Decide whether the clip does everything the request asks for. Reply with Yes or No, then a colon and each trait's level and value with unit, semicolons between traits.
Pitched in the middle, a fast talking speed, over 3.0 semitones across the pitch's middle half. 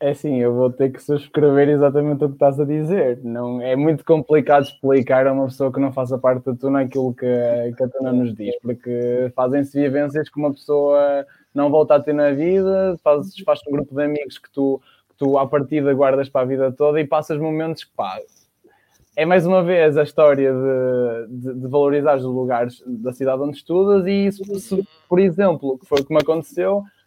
No: medium, 145 Hz; fast, 210 wpm; average, 2.7 semitones